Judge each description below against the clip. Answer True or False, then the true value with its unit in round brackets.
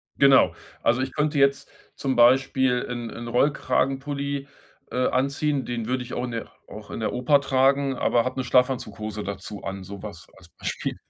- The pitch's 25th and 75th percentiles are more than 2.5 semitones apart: True (2.9 semitones)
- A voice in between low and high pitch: False (130 Hz)